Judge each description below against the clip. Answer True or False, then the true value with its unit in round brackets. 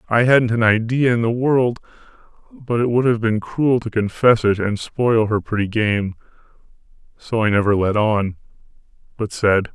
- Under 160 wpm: False (170 wpm)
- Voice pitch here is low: True (115 Hz)